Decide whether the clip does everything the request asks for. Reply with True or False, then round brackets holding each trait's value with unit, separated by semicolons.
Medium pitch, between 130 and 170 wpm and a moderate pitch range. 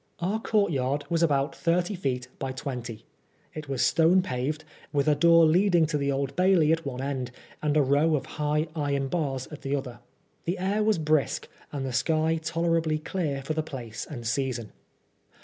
False (150 Hz; 185 wpm; 3.5 semitones)